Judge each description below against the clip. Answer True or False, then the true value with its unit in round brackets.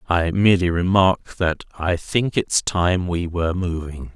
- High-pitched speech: False (90 Hz)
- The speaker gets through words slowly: False (160 wpm)